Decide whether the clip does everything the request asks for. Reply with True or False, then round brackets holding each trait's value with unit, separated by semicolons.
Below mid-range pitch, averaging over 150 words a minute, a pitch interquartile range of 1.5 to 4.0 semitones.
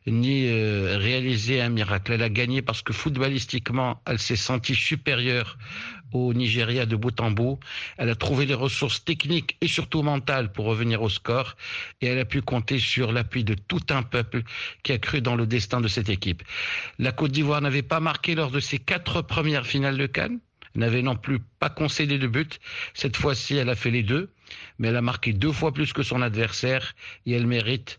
True (125 Hz; 205 wpm; 3.3 semitones)